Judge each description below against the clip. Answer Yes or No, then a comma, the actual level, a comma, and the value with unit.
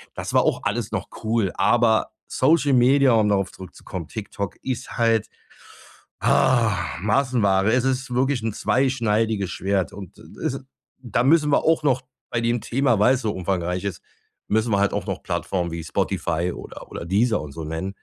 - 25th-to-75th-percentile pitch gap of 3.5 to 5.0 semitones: Yes, average, 4.7 semitones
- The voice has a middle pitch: No, low, 110 Hz